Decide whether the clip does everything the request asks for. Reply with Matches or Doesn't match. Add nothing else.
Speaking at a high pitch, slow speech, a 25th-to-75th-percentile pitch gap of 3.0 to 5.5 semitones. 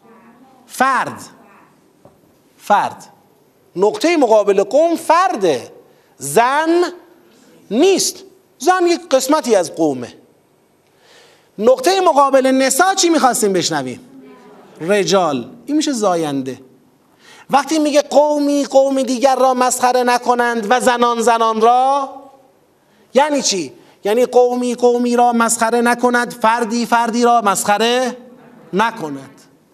Matches